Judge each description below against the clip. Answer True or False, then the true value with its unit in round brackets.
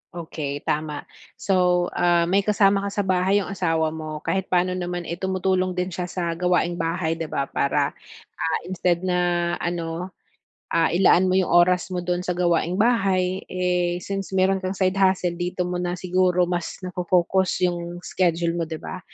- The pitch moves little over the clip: True (1.4 semitones)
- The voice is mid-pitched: True (180 Hz)